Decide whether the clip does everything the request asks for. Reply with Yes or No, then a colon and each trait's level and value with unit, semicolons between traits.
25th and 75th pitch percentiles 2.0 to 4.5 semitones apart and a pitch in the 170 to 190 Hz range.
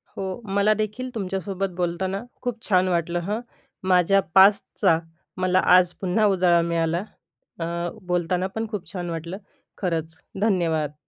Yes: narrow, 2.4 semitones; medium, 185 Hz